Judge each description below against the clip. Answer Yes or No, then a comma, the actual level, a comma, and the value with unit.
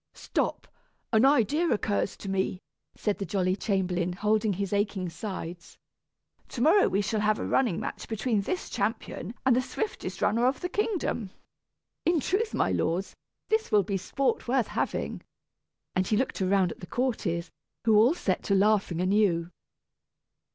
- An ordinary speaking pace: Yes, average, 160 wpm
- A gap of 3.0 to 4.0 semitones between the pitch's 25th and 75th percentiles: No, average, 4.7 semitones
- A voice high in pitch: Yes, high, 210 Hz